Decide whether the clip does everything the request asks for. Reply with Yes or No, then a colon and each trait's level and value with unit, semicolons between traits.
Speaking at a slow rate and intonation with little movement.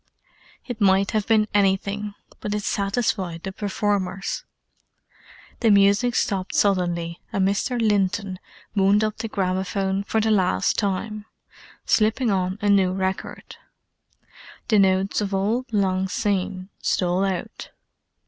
Yes: slow, 125 wpm; narrow, 1.8 semitones